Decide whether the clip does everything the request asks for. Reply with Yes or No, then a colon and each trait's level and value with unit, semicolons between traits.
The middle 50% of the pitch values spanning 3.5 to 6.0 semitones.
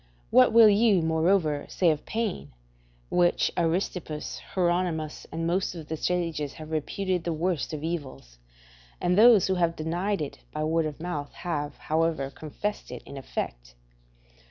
No: average, 2.9 semitones